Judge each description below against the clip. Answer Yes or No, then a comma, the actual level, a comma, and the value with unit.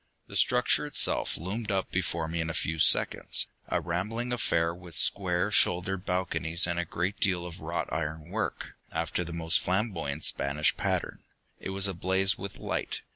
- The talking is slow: No, average, 170 wpm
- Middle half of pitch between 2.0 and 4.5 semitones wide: Yes, average, 2.7 semitones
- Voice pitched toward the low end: Yes, very low, 90 Hz